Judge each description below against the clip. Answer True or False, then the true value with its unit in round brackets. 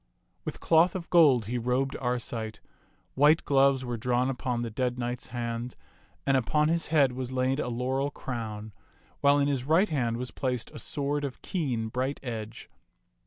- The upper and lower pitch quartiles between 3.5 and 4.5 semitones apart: False (2.8 semitones)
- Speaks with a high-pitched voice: False (130 Hz)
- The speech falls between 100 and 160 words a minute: False (170 wpm)